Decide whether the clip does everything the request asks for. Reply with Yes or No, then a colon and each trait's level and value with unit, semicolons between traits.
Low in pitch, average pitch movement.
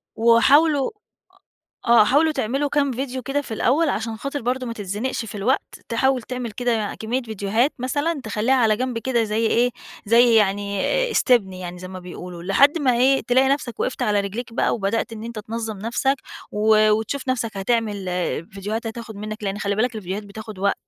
No: high, 230 Hz; average, 3.6 semitones